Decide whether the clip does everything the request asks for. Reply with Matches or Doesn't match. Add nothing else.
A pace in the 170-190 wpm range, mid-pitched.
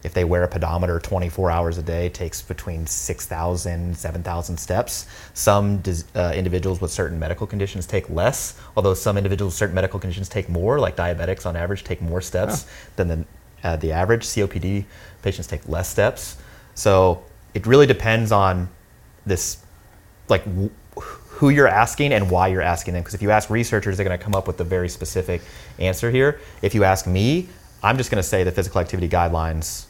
Doesn't match